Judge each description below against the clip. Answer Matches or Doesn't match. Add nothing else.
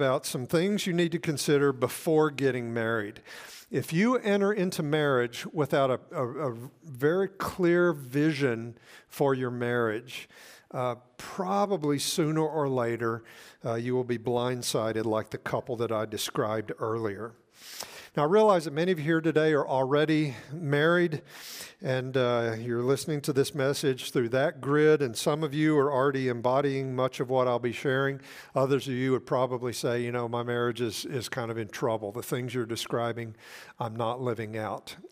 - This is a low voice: Matches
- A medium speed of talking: Matches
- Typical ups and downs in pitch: Matches